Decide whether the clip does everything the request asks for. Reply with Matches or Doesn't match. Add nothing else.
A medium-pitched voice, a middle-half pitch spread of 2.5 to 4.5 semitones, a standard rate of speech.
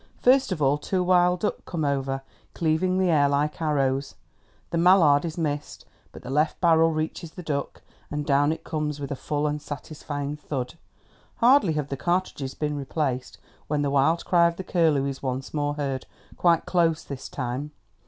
Matches